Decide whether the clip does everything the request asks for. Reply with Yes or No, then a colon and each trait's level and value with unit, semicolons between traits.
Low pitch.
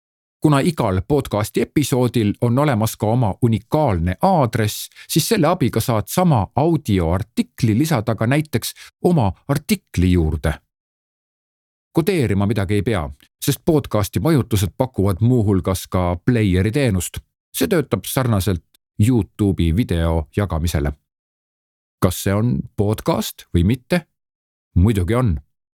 Yes: low, 110 Hz